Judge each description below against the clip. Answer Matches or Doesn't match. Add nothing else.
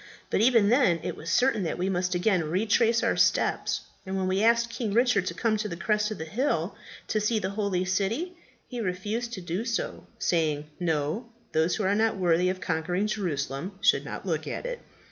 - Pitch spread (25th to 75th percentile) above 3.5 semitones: Matches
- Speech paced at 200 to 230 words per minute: Matches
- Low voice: Doesn't match